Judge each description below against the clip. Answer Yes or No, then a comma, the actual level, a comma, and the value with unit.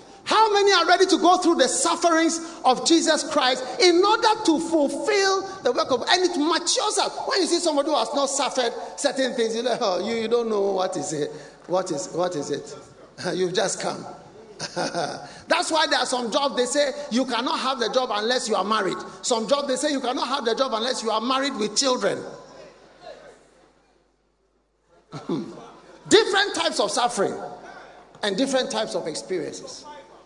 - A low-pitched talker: No, very high, 270 Hz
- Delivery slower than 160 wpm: No, average, 180 wpm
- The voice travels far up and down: Yes, wide, 6.2 semitones